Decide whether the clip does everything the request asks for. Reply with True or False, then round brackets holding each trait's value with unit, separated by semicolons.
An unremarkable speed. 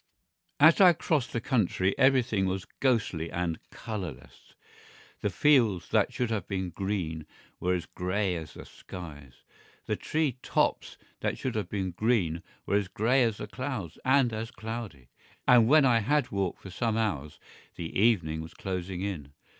True (160 wpm)